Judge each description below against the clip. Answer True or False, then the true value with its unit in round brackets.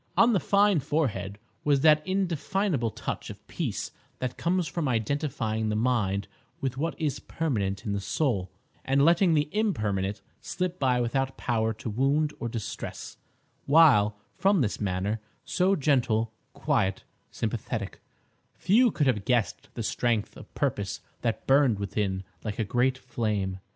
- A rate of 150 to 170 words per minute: False (140 wpm)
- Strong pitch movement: True (6.4 semitones)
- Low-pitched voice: True (125 Hz)